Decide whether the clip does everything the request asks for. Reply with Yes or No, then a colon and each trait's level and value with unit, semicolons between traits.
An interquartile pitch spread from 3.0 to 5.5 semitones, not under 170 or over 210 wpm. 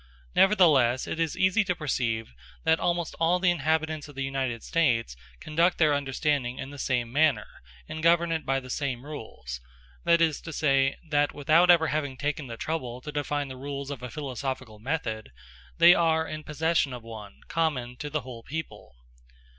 Yes: average, 4.0 semitones; average, 180 wpm